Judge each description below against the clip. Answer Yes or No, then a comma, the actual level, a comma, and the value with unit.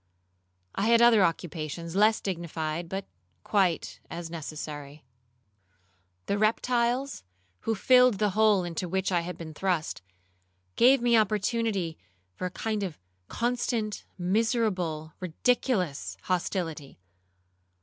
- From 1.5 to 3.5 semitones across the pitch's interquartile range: No, average, 5.1 semitones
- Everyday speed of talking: No, slow, 110 wpm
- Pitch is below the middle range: No, high, 190 Hz